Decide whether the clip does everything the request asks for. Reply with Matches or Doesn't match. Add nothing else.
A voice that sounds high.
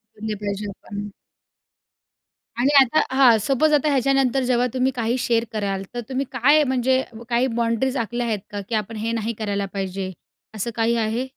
Matches